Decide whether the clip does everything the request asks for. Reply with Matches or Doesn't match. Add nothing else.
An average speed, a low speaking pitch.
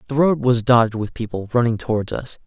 Doesn't match